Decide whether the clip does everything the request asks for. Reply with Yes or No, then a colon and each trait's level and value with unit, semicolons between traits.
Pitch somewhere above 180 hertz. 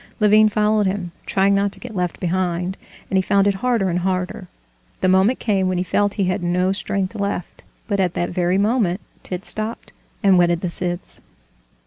Yes: high, 190 Hz